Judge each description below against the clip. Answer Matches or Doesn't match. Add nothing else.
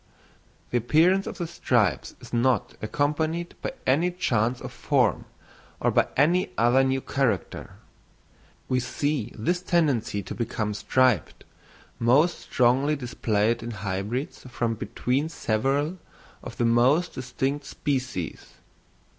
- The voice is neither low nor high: Doesn't match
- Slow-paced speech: Matches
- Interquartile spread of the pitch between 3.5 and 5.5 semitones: Matches